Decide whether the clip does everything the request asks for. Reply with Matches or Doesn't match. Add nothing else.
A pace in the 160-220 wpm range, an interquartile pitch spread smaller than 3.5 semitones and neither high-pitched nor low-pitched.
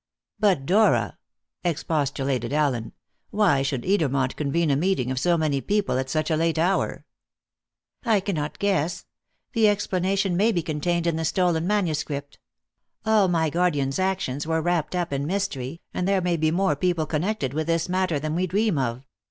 Doesn't match